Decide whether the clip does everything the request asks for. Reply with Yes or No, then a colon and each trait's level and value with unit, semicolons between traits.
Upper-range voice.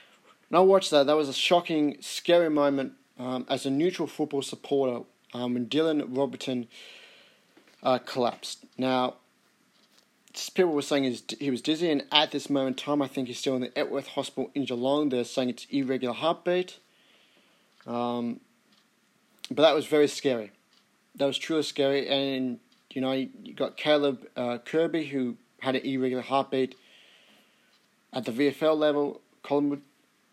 No: medium, 140 Hz